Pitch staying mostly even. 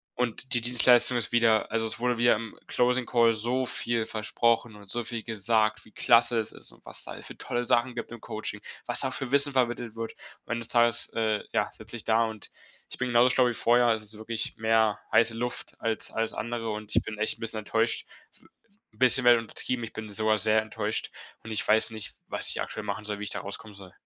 Yes: narrow, 1.7 semitones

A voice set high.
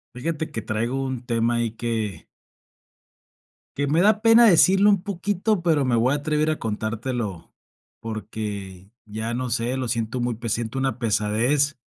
No: low, 120 Hz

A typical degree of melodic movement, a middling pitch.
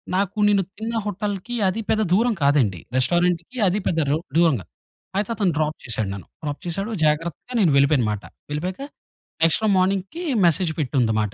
No: wide, 5.9 semitones; medium, 175 Hz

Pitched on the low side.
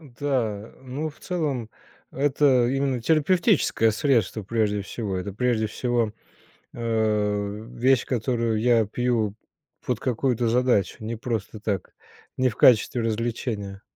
Yes: low, 115 Hz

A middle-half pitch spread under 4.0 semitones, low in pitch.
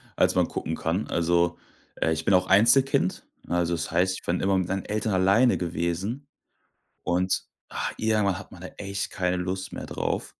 Yes: narrow, 2.4 semitones; very low, 95 Hz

